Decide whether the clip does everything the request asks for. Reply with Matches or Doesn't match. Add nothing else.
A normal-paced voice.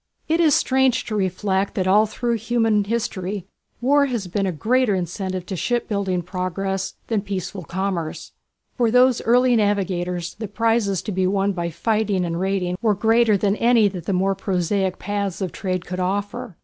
Matches